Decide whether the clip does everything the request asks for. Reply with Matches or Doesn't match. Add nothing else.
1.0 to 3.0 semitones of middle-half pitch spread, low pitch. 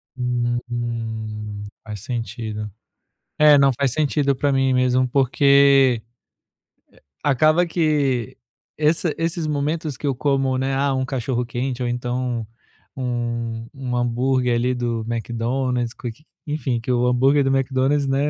Matches